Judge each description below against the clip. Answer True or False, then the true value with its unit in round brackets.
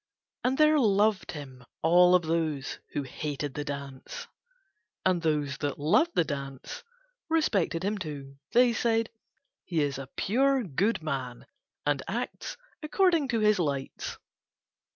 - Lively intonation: True (8.0 semitones)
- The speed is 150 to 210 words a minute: False (135 wpm)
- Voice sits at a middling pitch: True (165 Hz)